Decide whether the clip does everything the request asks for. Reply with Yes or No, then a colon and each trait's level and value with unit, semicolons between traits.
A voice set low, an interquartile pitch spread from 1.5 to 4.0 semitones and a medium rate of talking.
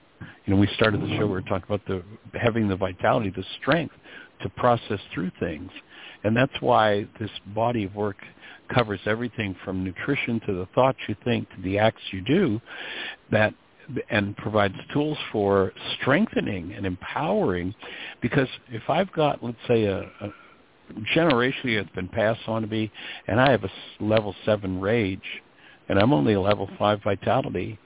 Yes: low, 105 Hz; average, 2.8 semitones; average, 170 wpm